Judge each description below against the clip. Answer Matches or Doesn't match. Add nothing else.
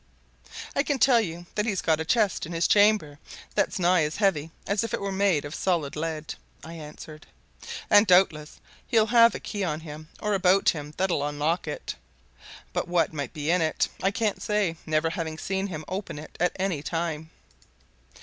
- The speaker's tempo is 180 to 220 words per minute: Matches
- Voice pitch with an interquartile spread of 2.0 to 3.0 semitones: Doesn't match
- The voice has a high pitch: Doesn't match